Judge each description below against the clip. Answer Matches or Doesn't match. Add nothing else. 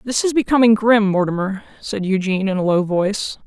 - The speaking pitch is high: Matches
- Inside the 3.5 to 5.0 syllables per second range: Doesn't match